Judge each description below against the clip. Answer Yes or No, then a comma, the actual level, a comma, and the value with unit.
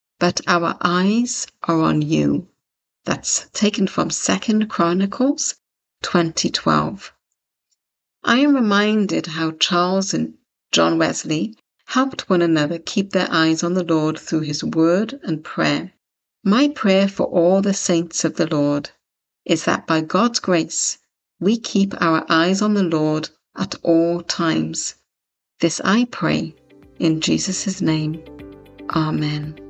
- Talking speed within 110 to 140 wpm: Yes, slow, 135 wpm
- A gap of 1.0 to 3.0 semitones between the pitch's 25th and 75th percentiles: No, average, 3.9 semitones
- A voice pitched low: No, medium, 170 Hz